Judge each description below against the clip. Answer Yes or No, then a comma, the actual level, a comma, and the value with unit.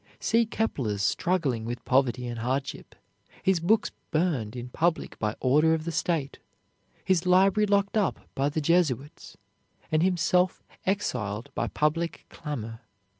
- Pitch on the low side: No, medium, 155 Hz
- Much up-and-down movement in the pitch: Yes, wide, 6.3 semitones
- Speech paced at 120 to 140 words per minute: Yes, slow, 135 wpm